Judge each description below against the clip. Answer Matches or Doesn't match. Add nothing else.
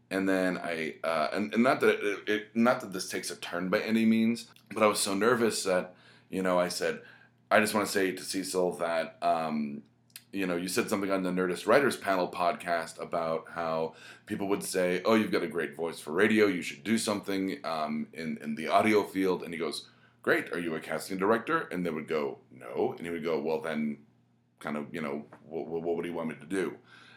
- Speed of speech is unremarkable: Doesn't match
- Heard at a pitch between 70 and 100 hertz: Matches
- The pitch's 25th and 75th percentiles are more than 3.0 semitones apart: Matches